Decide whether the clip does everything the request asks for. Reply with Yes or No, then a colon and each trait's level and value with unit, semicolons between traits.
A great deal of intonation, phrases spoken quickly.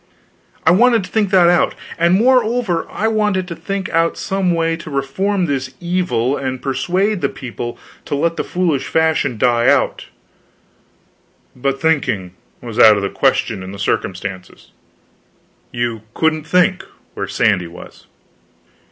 No: wide, 7.1 semitones; average, 145 wpm